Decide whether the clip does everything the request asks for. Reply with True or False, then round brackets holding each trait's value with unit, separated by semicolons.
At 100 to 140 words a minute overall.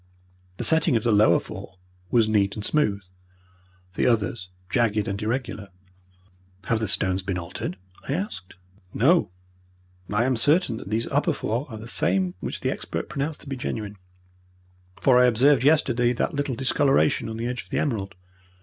False (170 wpm)